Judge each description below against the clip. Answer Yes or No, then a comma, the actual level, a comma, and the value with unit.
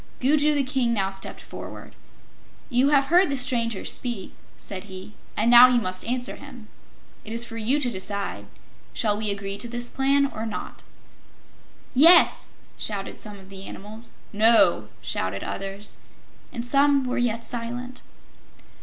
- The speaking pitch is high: Yes, high, 230 Hz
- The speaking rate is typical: Yes, average, 155 wpm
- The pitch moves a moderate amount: Yes, average, 4.2 semitones